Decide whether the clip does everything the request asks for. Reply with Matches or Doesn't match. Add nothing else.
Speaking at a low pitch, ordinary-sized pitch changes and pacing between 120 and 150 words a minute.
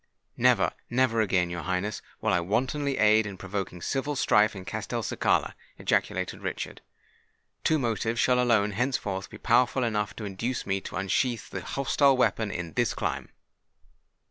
Matches